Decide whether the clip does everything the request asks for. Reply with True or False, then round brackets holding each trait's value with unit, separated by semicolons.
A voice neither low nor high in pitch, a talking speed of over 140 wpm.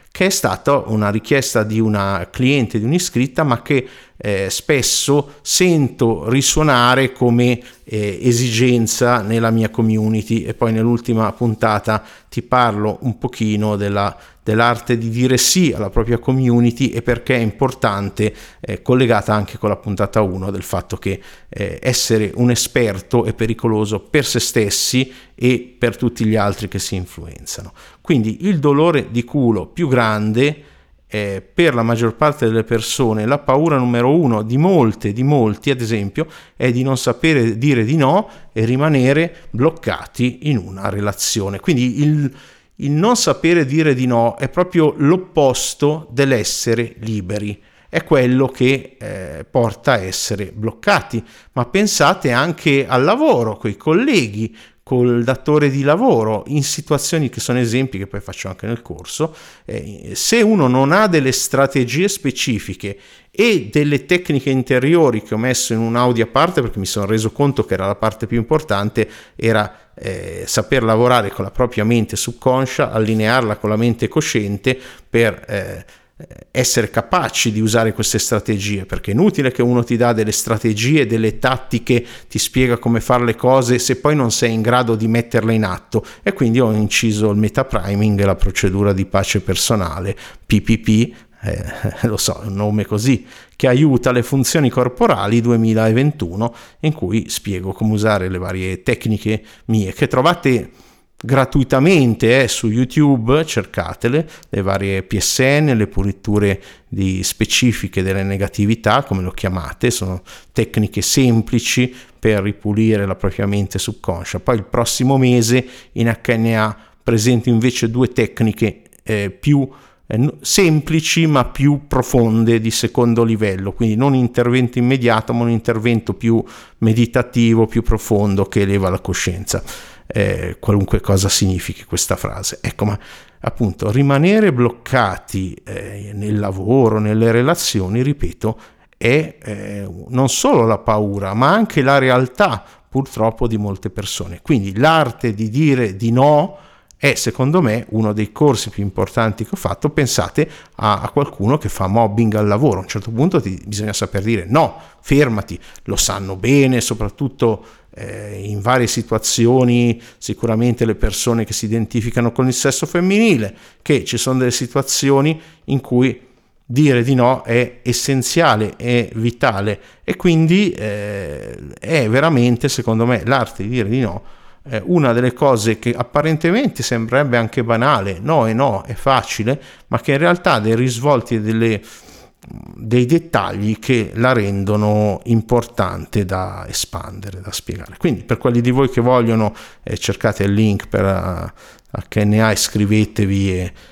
False (115 Hz; 150 wpm)